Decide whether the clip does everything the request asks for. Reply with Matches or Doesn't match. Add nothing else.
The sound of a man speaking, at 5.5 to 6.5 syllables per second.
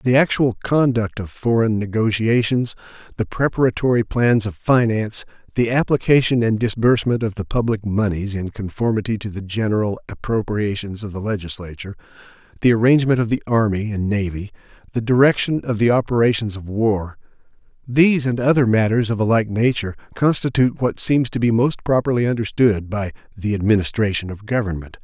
Matches